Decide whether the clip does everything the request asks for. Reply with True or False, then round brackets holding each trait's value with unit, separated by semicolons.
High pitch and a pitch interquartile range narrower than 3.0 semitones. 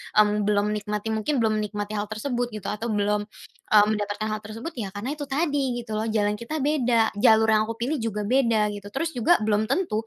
True (215 Hz; 2.6 semitones)